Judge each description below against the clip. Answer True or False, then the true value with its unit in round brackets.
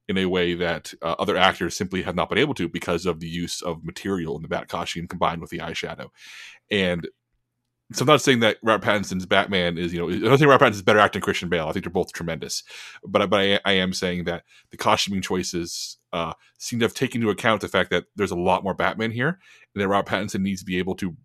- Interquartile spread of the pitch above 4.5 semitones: False (3.1 semitones)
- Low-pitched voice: True (95 Hz)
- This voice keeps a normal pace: False (250 wpm)